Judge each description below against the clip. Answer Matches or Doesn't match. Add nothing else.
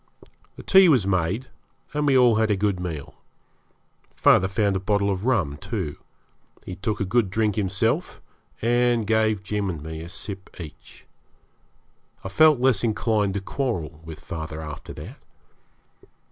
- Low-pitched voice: Matches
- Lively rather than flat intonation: Doesn't match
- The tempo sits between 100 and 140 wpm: Doesn't match